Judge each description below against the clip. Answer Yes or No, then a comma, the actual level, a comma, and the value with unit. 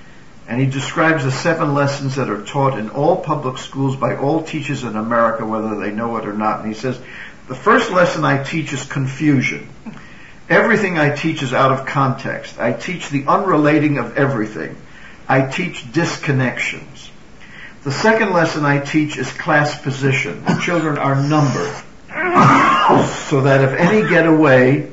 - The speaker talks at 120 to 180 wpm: Yes, average, 165 wpm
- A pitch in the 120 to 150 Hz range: Yes, medium, 140 Hz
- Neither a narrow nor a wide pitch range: Yes, average, 3.0 semitones